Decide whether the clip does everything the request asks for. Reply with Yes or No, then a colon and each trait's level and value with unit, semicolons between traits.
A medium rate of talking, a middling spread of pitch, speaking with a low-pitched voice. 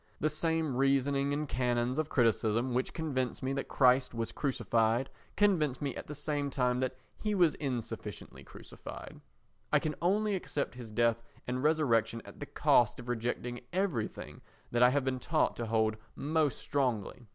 Yes: average, 165 wpm; average, 3.8 semitones; low, 130 Hz